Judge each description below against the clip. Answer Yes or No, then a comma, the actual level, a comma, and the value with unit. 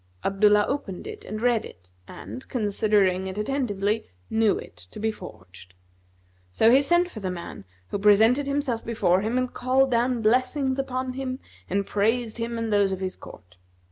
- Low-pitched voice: No, high, 220 Hz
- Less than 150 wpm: No, average, 170 wpm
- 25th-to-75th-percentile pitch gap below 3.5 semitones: No, average, 4.5 semitones